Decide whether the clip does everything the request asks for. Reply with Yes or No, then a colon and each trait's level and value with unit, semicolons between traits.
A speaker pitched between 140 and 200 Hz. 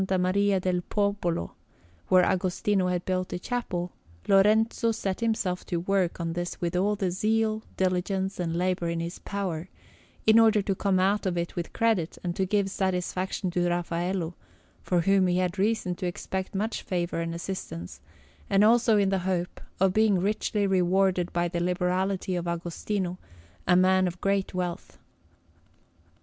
Yes: medium, 185 Hz